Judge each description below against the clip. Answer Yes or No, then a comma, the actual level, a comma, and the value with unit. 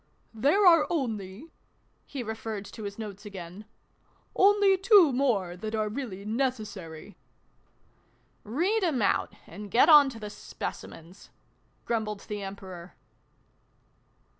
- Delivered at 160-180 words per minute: No, slow, 135 wpm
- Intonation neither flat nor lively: No, wide, 5.9 semitones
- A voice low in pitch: No, high, 220 Hz